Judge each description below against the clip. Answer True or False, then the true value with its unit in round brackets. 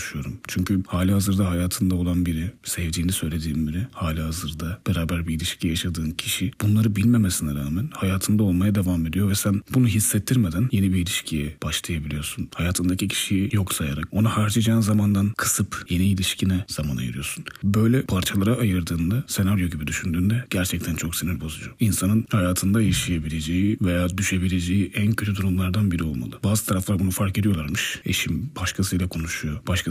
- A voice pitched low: True (95 Hz)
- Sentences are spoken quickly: True (145 wpm)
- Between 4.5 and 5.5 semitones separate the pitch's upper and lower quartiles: False (3.4 semitones)